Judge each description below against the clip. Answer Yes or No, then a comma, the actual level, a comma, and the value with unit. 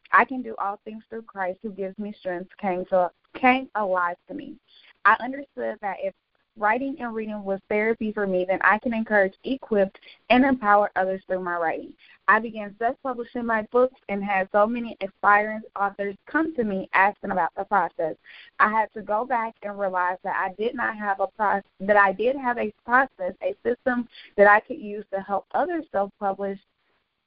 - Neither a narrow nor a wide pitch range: Yes, average, 3.2 semitones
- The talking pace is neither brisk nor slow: Yes, average, 190 wpm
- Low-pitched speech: No, high, 205 Hz